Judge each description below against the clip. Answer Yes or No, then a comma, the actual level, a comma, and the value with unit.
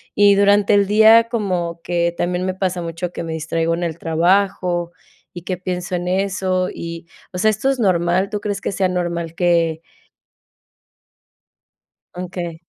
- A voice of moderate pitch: Yes, medium, 180 Hz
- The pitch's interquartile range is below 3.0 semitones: Yes, narrow, 2.5 semitones